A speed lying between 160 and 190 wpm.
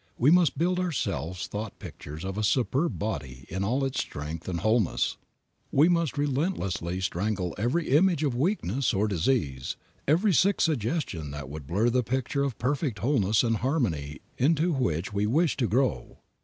Yes: average, 165 wpm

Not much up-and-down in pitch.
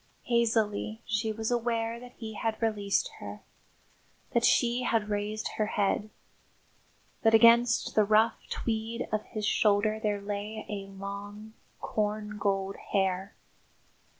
Yes: narrow, 1.7 semitones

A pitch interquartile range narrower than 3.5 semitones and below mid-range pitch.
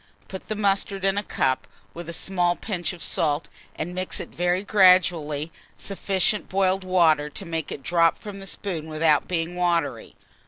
No: average, 2.8 semitones; medium, 175 Hz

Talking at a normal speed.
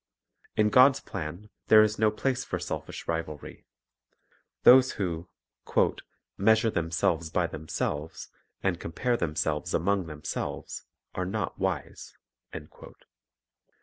No: slow, 105 wpm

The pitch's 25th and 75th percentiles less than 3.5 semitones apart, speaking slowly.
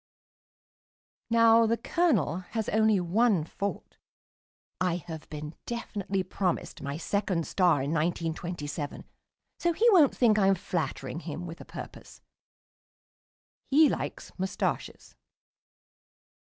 No: wide, 5.4 semitones; slow, 110 wpm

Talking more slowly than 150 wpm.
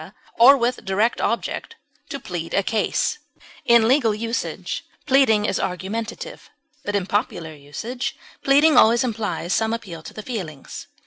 Yes: average, 140 wpm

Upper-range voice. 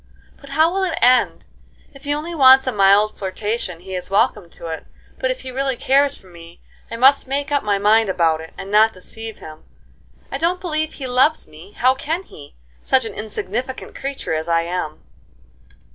Yes: high, 230 Hz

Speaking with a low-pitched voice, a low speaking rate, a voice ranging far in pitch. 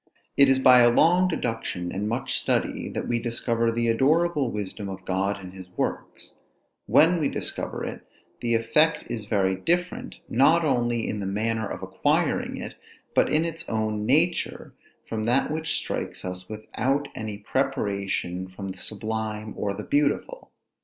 No: low, 115 Hz; average, 160 wpm; wide, 5.7 semitones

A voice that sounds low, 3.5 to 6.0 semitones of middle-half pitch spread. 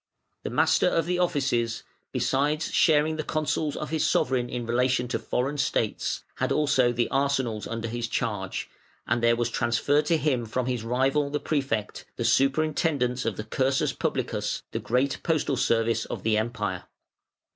Yes: low, 125 Hz; average, 4.0 semitones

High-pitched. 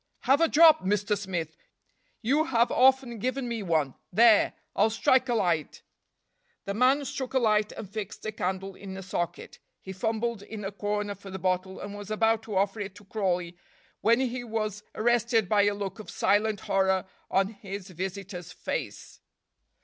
Yes: high, 205 Hz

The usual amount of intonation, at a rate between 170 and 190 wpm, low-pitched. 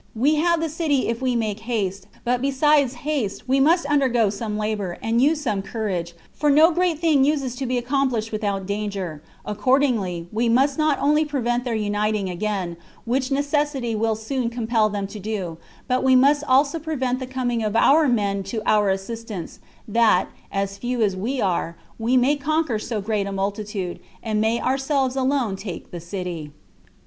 No: average, 4.9 semitones; average, 180 wpm; high, 235 Hz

